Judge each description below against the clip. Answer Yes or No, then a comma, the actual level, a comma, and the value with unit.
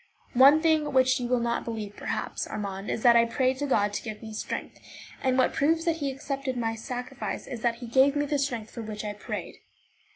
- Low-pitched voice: No, very high, 250 Hz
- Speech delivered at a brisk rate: Yes, fast, 220 wpm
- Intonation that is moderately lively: Yes, average, 3.4 semitones